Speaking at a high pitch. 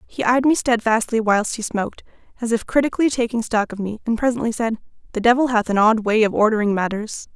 Yes: high, 225 Hz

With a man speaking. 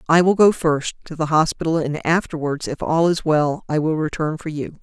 No: female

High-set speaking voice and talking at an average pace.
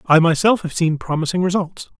No: medium, 170 Hz; average, 180 wpm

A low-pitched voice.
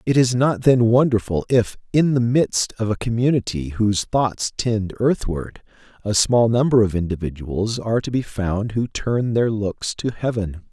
Yes: low, 110 Hz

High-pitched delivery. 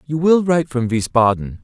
No: low, 135 Hz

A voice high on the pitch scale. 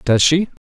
No: medium, 150 Hz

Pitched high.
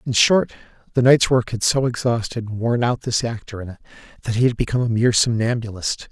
No: low, 115 Hz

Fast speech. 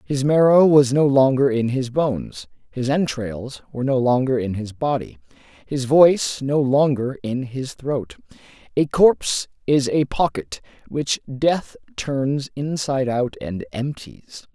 No: average, 145 wpm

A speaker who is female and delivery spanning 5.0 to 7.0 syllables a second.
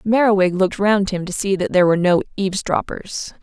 Yes: female; 6.0 syllables/s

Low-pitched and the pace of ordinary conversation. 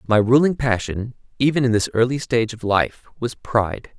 Yes: low, 120 Hz; average, 180 wpm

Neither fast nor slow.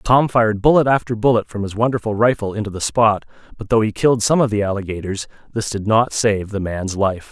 No: fast, 220 wpm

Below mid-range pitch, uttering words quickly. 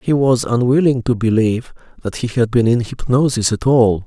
No: low, 120 Hz; average, 190 wpm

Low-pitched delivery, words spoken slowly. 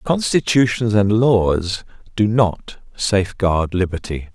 Yes: low, 105 Hz; slow, 95 wpm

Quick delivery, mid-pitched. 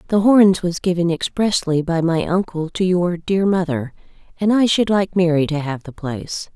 No: average, 190 wpm; medium, 175 Hz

